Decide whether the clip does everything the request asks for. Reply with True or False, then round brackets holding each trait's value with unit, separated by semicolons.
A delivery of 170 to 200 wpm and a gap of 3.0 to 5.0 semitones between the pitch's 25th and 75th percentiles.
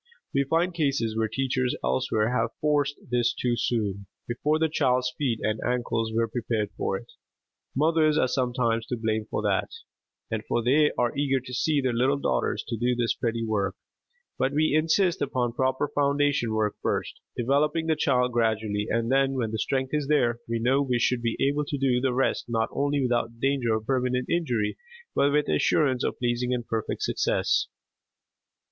True (180 wpm; 3.5 semitones)